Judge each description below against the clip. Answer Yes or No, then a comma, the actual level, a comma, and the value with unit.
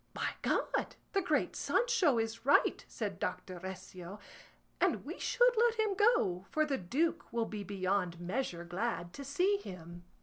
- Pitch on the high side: Yes, high, 230 Hz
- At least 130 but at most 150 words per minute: No, average, 160 wpm